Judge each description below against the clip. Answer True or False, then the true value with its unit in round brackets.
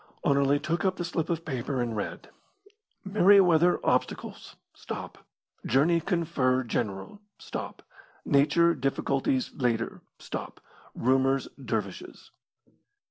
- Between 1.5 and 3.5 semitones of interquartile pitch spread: False (5.0 semitones)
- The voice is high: False (140 Hz)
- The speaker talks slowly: True (100 wpm)